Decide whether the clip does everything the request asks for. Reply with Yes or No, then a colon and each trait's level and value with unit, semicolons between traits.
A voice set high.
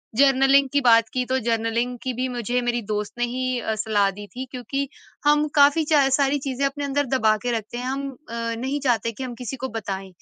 Yes: very high, 250 Hz